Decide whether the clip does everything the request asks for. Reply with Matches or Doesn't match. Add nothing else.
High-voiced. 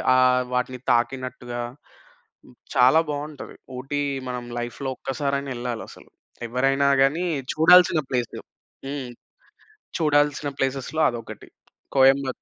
Doesn't match